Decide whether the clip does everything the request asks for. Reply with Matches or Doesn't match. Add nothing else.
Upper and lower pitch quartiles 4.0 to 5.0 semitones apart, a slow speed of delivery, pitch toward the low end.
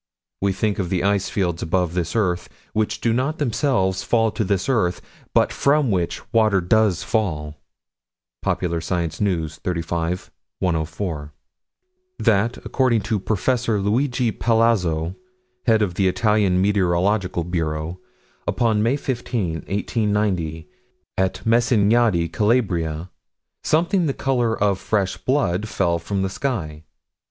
Matches